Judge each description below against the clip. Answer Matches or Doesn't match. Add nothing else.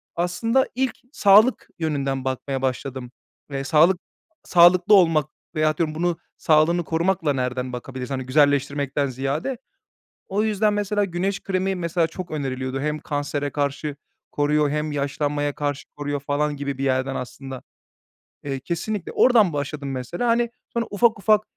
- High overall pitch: Doesn't match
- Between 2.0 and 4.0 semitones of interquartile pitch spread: Doesn't match